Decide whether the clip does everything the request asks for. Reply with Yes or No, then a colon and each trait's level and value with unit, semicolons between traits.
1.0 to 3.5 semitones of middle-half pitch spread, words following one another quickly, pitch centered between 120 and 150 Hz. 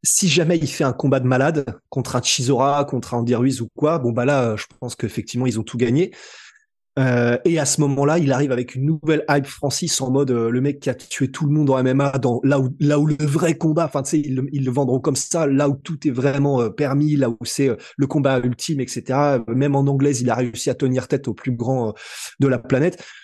Yes: narrow, 2.6 semitones; fast, 255 wpm; medium, 140 Hz